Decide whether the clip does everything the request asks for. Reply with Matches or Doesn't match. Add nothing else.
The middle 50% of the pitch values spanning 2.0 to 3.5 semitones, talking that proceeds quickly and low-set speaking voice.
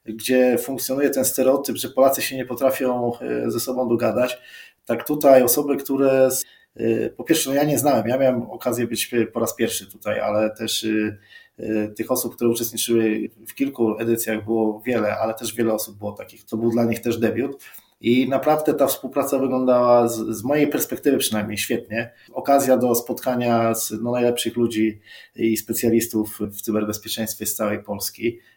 Matches